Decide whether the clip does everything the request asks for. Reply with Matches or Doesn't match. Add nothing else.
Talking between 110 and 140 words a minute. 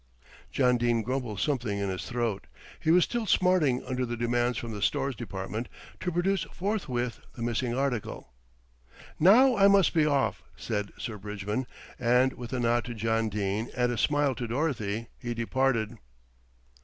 Doesn't match